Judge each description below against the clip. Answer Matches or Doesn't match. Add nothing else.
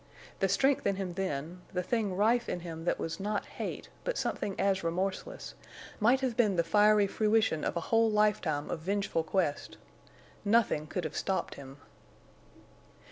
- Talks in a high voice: Matches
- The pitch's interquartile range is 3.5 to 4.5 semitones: Matches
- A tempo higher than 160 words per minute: Doesn't match